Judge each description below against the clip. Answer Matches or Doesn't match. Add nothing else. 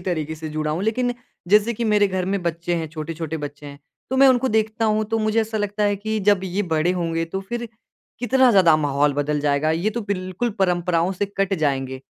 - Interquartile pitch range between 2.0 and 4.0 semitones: Doesn't match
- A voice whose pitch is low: Doesn't match